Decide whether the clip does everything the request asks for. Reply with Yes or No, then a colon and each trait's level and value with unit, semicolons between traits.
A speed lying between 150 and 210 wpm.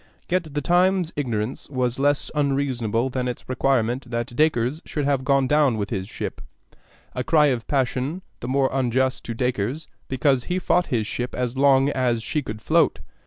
Yes: average, 175 wpm